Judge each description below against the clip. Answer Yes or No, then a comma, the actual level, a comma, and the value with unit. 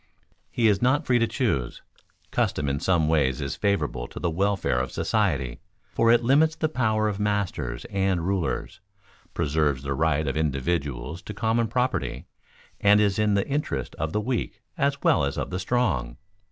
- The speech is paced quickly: No, average, 175 wpm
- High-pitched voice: No, very low, 95 Hz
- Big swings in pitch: Yes, wide, 7.9 semitones